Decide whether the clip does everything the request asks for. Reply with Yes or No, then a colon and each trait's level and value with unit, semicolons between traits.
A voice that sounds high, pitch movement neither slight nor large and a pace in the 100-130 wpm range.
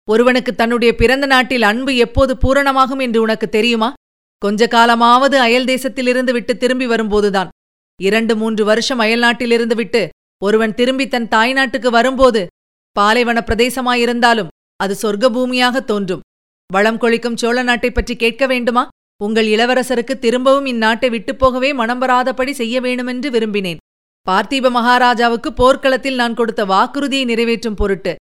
No: high, 240 Hz; narrow, 2.3 semitones; average, 125 wpm